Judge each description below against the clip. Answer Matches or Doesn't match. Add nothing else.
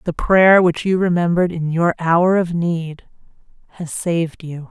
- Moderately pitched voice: Matches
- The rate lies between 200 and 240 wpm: Doesn't match